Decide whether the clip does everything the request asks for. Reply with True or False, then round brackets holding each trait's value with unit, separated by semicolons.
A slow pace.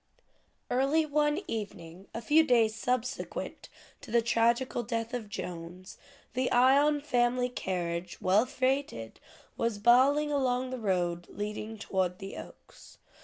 True (125 wpm)